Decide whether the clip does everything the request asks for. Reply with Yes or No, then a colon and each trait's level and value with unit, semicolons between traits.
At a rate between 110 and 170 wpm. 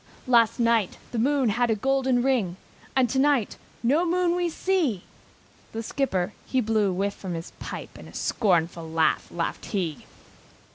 Yes: average, 160 wpm